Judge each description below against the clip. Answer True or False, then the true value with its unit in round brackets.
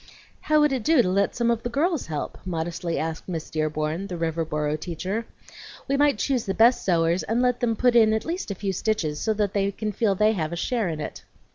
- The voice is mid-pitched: False (200 Hz)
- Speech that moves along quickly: True (235 wpm)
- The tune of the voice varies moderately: False (6.1 semitones)